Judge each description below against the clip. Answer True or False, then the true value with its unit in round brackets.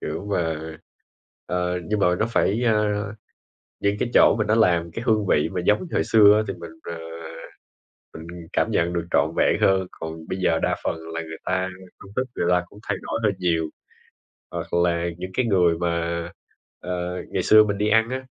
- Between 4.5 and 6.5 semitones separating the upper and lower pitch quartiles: False (3.8 semitones)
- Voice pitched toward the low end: True (90 Hz)